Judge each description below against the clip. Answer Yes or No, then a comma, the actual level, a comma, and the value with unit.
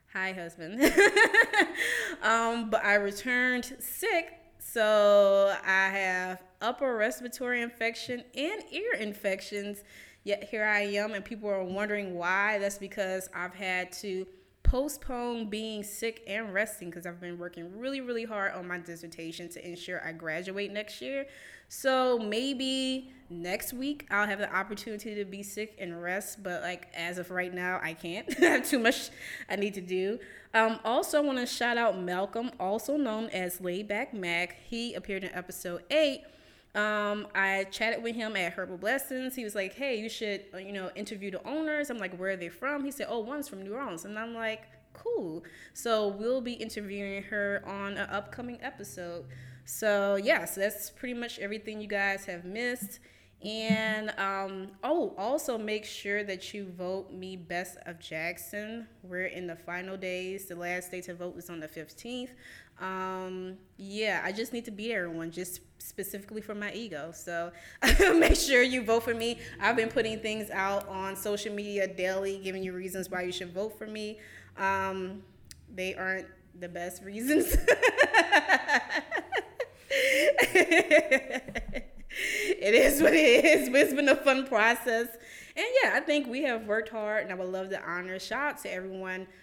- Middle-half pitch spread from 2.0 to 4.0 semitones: No, average, 4.5 semitones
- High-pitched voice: Yes, high, 205 Hz